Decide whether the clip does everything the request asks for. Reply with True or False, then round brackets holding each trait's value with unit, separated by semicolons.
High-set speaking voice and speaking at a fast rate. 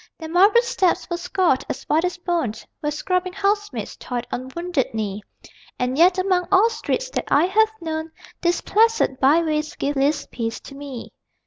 False (335 Hz; 175 wpm)